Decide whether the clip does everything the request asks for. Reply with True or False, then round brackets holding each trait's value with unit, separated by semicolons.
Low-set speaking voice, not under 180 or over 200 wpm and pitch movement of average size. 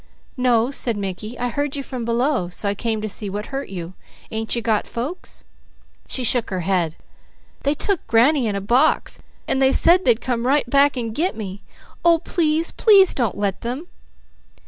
False (240 Hz; 190 wpm; 4.9 semitones)